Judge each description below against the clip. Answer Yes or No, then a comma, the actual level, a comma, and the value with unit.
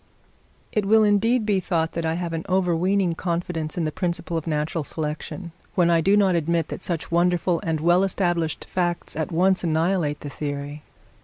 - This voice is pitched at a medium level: Yes, medium, 170 Hz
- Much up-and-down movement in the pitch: No, narrow, 2.5 semitones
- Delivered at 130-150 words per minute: No, average, 180 wpm